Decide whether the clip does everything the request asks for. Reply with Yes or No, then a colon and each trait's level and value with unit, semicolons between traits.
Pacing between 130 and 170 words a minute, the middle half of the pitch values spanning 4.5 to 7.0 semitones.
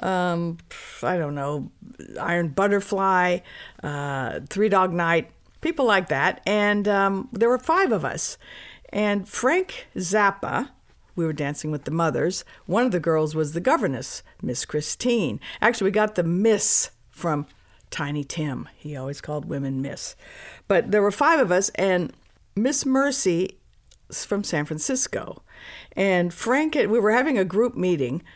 Yes: average, 150 wpm; average, 5.3 semitones